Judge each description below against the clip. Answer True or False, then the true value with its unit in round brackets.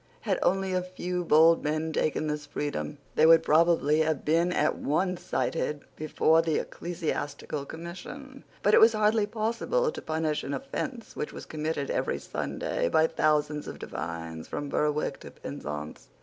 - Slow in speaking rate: False (160 wpm)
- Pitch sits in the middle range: True (160 Hz)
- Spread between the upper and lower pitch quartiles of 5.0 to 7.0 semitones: False (3.4 semitones)